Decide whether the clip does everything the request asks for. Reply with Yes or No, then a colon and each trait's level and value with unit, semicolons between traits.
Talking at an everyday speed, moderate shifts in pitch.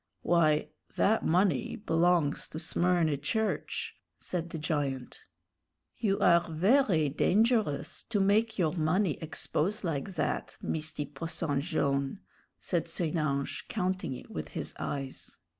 No: slow, 125 wpm; average, 4.4 semitones